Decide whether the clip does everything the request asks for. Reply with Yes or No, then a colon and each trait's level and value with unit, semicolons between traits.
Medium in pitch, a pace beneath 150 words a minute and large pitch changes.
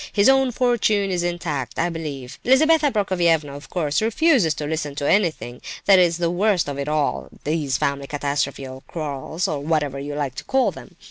No: medium, 160 Hz; average, 185 wpm; wide, 5.8 semitones